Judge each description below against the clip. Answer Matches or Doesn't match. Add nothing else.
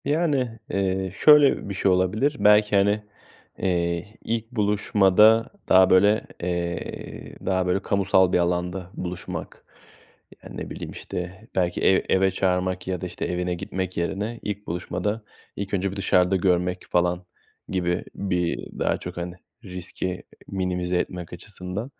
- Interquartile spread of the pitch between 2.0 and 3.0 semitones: Matches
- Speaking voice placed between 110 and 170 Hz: Doesn't match